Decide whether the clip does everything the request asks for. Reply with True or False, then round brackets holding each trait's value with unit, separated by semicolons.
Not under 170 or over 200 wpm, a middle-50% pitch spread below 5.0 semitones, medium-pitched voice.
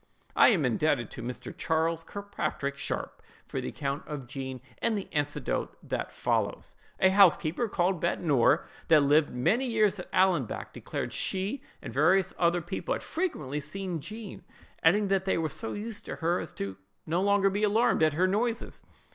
False (175 wpm; 5.3 semitones; 175 Hz)